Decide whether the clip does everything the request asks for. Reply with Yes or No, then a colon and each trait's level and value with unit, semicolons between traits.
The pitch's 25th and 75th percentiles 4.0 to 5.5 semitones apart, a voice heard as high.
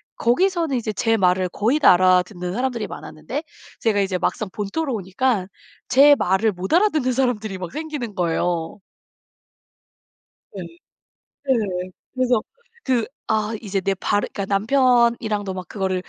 Yes: average, 5.2 semitones; high, 215 Hz